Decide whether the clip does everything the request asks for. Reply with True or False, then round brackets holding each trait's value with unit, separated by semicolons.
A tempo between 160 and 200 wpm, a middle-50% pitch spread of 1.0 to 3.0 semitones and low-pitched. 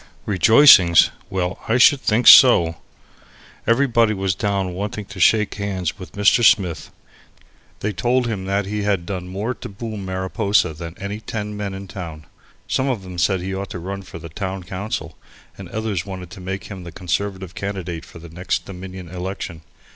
True (175 wpm; 2.5 semitones; 95 Hz)